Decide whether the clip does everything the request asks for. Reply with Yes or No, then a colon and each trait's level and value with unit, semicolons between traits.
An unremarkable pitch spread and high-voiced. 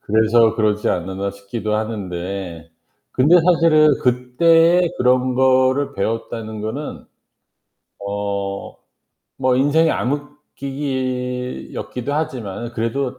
No: average, 4.7 semitones; low, 125 Hz